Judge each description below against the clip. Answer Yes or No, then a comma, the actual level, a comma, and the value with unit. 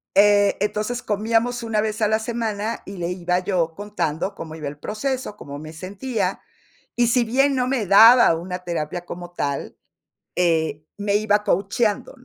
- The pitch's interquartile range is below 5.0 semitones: Yes, average, 4.3 semitones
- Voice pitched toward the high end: Yes, high, 205 Hz